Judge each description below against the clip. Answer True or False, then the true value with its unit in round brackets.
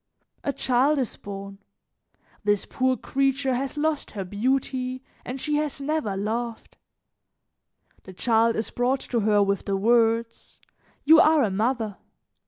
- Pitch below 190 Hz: False (240 Hz)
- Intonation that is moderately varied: True (4.4 semitones)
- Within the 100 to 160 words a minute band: True (140 wpm)